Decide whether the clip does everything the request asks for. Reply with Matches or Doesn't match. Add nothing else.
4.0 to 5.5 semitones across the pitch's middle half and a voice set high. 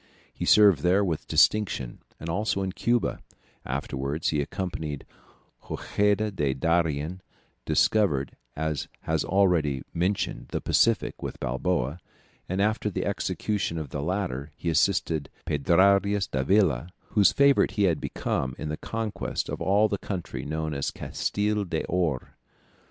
Doesn't match